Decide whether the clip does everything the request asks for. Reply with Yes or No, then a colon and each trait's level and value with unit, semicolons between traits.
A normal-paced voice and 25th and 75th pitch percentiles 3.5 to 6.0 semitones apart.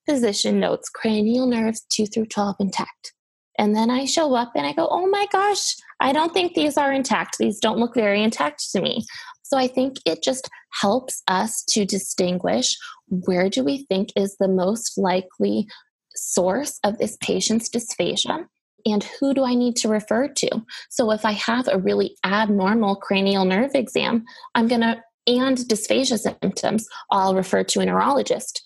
Yes: average, 175 wpm; average, 4.8 semitones